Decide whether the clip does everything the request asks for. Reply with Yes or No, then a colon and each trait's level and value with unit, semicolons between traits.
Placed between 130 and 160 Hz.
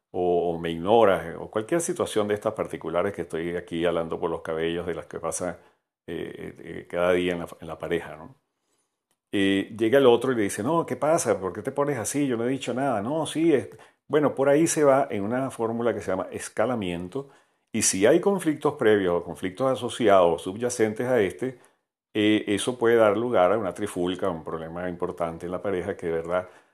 No: low, 105 Hz